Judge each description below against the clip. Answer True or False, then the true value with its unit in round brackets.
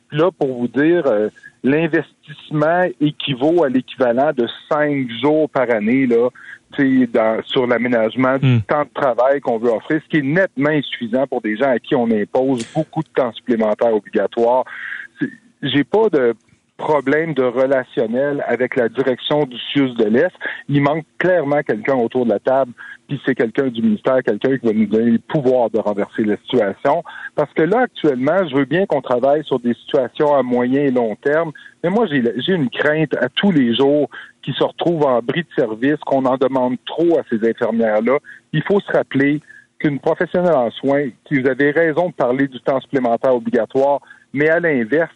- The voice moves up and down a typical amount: True (3.8 semitones)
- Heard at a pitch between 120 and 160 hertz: True (140 Hz)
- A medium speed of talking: True (190 wpm)